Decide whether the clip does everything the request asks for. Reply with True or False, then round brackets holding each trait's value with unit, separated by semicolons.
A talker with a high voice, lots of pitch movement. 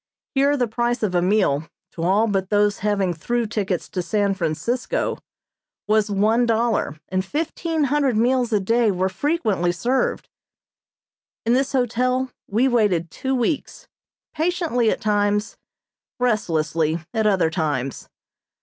False (215 Hz; 4.8 semitones)